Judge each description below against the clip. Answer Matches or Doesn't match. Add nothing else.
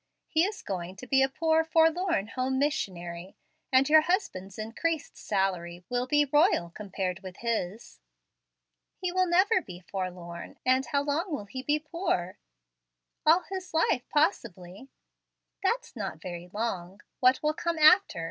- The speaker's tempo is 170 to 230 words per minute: Doesn't match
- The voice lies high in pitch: Matches